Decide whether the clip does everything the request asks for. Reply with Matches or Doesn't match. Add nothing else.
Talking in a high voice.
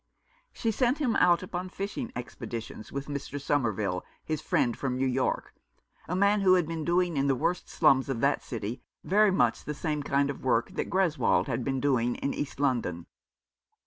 Doesn't match